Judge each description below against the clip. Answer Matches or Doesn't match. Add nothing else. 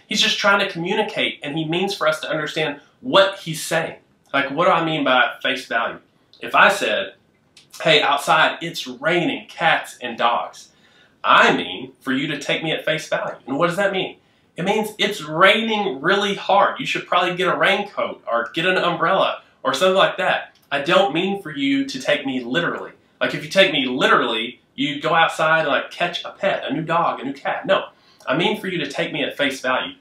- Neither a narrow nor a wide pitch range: Matches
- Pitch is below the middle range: Doesn't match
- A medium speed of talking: Doesn't match